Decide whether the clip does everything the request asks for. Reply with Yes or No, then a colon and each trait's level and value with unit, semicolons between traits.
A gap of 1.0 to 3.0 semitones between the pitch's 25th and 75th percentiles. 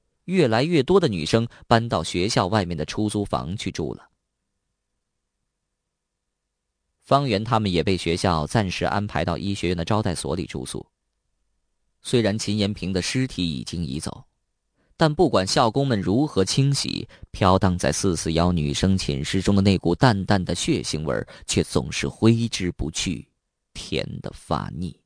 No: average, 4.3 semitones